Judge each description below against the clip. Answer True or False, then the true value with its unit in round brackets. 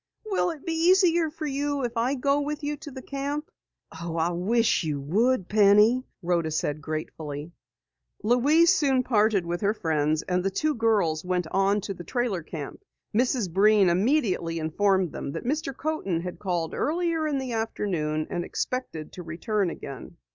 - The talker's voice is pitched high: True (210 Hz)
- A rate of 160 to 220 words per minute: True (170 wpm)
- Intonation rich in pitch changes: True (8.3 semitones)